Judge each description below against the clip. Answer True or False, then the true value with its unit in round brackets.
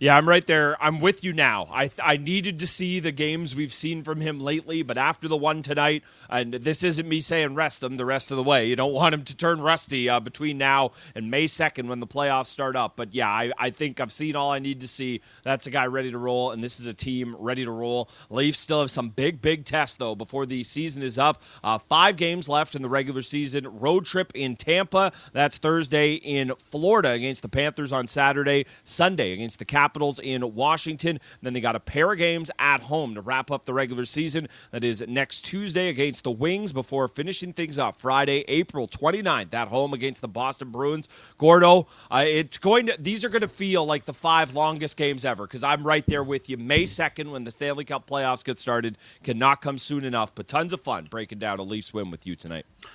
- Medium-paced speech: False (230 wpm)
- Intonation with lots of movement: False (3.6 semitones)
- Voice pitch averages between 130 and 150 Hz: True (140 Hz)